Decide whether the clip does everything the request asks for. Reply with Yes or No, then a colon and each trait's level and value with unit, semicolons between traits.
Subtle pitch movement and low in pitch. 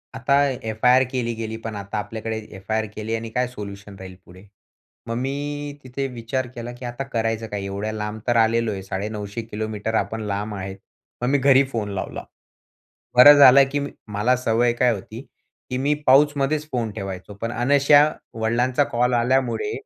No: average, 3.6 semitones; low, 115 Hz